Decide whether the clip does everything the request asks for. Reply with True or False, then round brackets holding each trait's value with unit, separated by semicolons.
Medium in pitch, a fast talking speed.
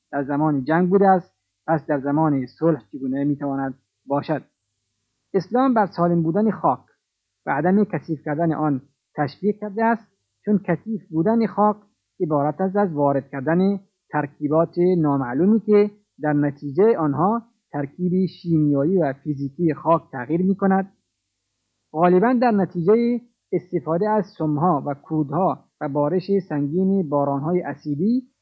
False (165 Hz; 130 wpm)